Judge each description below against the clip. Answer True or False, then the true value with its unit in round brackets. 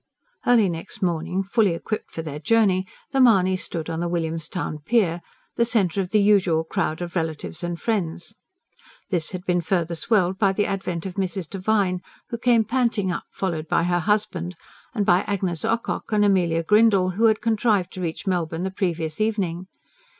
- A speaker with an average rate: True (180 wpm)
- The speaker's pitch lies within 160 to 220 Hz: True (185 Hz)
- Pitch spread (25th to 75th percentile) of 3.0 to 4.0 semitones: True (3.6 semitones)